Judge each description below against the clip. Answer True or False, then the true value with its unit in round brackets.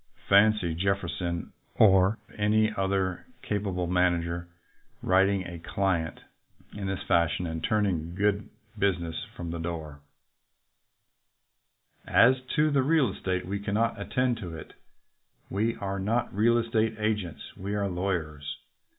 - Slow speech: True (125 wpm)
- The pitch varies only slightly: False (3.6 semitones)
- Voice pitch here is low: True (95 Hz)